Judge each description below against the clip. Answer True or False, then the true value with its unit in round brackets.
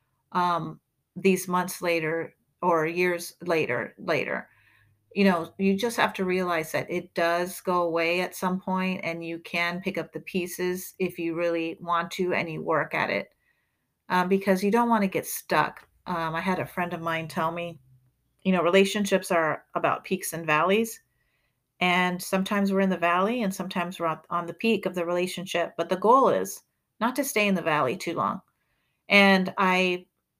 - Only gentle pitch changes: True (2.1 semitones)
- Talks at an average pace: True (185 wpm)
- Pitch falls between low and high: True (175 Hz)